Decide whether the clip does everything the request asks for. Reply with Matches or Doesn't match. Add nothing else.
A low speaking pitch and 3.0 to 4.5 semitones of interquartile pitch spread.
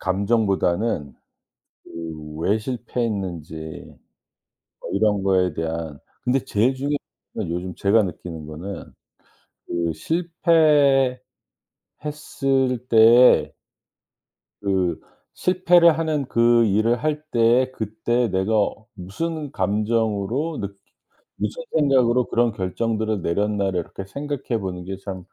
Doesn't match